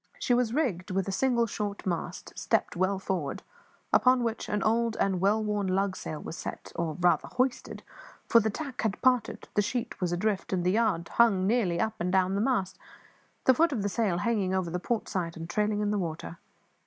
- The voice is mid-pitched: No, high, 200 Hz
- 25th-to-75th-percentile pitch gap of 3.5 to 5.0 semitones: Yes, average, 4.0 semitones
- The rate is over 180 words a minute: Yes, fast, 205 wpm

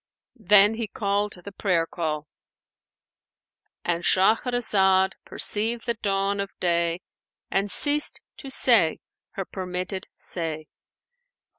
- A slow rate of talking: Yes, slow, 100 wpm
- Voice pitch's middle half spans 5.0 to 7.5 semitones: No, average, 3.3 semitones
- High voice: Yes, high, 195 Hz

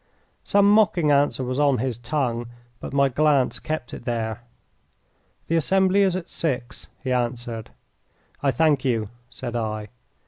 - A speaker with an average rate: Yes, average, 145 wpm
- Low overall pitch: Yes, low, 130 Hz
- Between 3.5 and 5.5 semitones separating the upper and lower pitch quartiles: Yes, average, 4.6 semitones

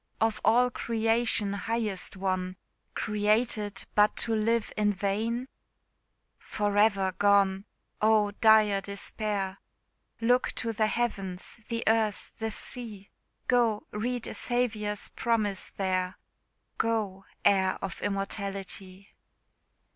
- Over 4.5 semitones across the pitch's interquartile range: No, narrow, 2.4 semitones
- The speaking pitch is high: Yes, high, 210 Hz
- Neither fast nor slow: No, slow, 105 wpm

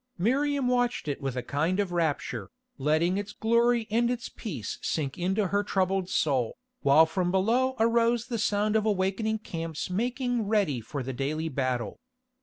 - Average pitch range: No, wide, 6.9 semitones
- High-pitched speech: Yes, high, 195 Hz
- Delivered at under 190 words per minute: Yes, average, 165 wpm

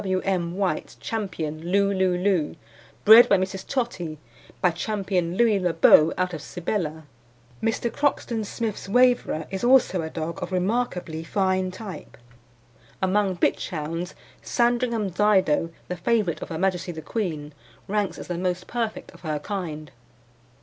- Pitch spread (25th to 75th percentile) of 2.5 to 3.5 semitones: No, average, 3.9 semitones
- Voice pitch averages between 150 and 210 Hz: Yes, medium, 185 Hz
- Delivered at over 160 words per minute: No, average, 150 wpm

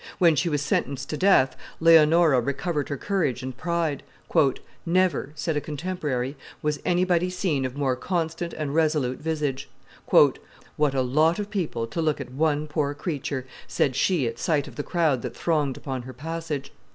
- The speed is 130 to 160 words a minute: No, average, 170 wpm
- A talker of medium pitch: Yes, medium, 150 Hz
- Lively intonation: No, average, 3.6 semitones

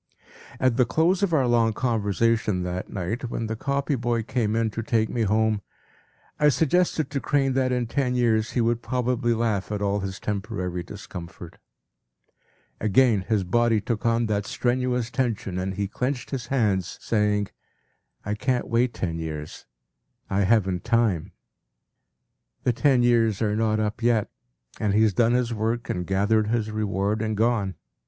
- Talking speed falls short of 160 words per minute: No, average, 165 wpm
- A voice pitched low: Yes, low, 115 Hz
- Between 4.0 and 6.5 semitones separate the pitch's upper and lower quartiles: No, average, 3.0 semitones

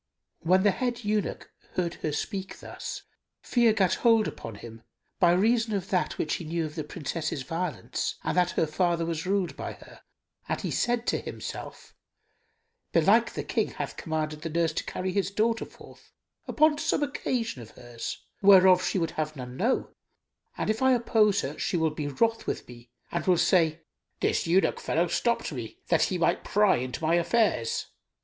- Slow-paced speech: No, average, 185 wpm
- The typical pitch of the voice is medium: Yes, medium, 175 Hz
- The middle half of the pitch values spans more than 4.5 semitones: Yes, average, 5.2 semitones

